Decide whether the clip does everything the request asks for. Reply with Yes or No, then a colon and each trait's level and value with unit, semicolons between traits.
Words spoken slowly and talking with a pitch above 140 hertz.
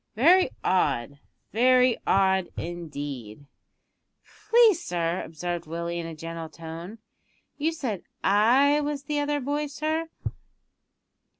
Yes: slow, 110 wpm; high, 190 Hz